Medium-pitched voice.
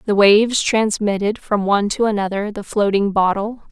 No: high, 205 Hz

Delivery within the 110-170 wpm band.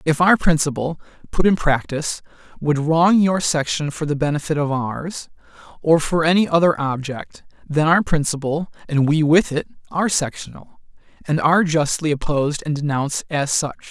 Yes: average, 160 wpm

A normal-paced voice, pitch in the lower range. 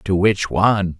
Yes: average, 180 wpm; very low, 95 Hz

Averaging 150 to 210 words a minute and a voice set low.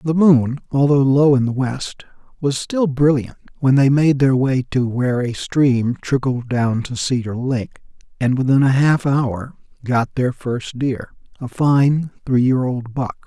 Yes: average, 175 wpm; low, 130 Hz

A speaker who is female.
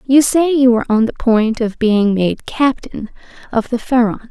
Yes: female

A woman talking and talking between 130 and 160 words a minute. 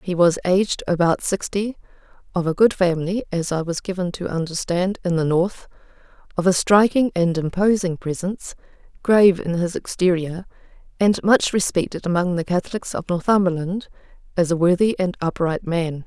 Yes: female; average, 150 wpm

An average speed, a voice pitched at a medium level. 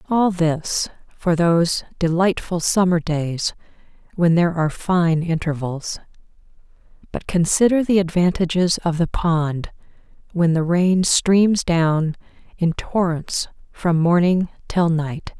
No: slow, 115 wpm; medium, 170 Hz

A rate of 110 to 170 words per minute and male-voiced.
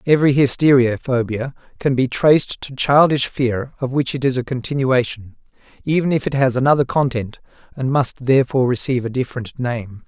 Yes: average, 165 wpm; male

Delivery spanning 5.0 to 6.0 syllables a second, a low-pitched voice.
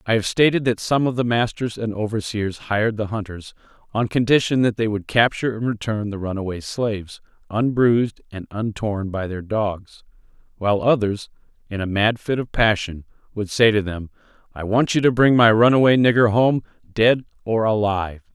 Yes: 5.2 syllables/s; low, 110 Hz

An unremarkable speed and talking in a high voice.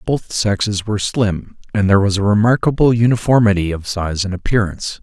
No: average, 165 wpm; low, 105 Hz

